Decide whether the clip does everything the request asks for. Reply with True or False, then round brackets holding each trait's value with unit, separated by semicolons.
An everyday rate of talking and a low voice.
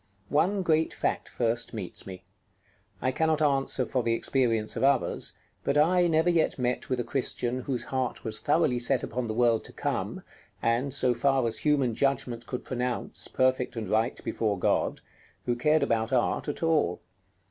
True (175 wpm; 125 Hz)